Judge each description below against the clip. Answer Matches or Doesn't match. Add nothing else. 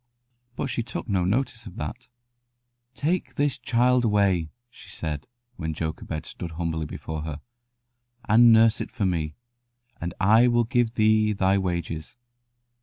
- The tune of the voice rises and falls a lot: Matches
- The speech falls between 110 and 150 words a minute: Matches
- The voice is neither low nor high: Doesn't match